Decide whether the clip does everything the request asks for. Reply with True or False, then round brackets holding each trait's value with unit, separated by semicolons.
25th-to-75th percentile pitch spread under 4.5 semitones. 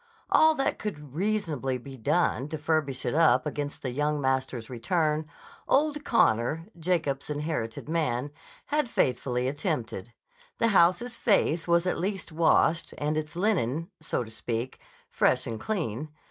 False (5.1 semitones)